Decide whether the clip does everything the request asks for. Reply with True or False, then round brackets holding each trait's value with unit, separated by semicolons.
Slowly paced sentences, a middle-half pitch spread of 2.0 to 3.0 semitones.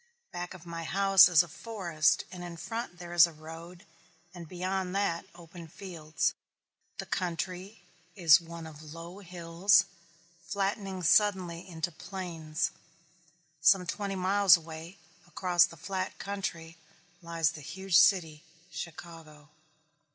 True (130 wpm; 2.5 semitones)